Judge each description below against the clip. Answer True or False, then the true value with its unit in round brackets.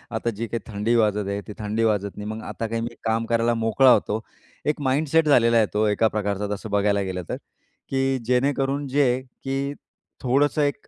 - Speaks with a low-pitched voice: True (115 Hz)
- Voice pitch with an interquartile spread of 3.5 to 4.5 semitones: True (4.2 semitones)